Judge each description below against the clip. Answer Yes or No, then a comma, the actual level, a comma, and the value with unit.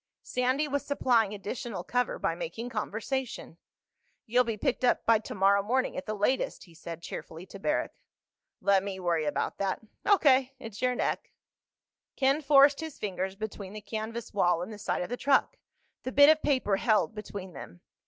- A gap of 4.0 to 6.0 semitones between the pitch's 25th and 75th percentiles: Yes, average, 5.0 semitones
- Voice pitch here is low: No, high, 220 Hz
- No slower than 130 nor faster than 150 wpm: No, average, 175 wpm